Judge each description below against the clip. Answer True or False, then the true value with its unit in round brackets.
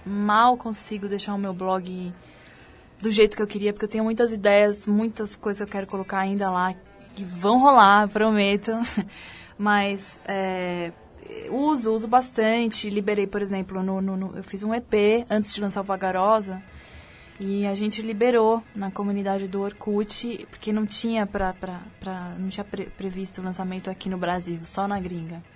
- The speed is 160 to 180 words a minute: True (175 wpm)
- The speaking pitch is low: False (200 Hz)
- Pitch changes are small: True (2.2 semitones)